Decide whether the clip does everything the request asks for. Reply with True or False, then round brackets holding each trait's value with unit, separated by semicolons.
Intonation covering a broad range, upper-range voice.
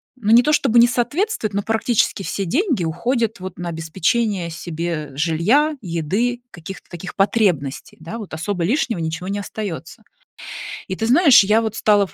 True (5.7 semitones; 200 Hz)